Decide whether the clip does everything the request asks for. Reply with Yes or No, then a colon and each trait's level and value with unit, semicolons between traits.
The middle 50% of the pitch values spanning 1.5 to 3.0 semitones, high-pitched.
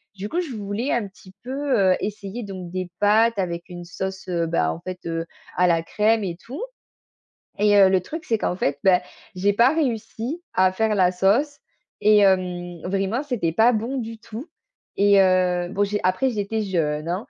No: average, 3.7 semitones; high, 200 Hz